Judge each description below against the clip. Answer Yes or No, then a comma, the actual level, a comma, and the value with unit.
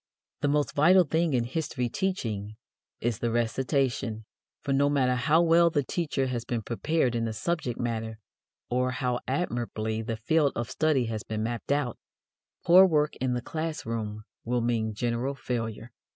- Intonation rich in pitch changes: No, average, 4.3 semitones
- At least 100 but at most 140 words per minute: No, average, 165 wpm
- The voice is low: Yes, low, 125 Hz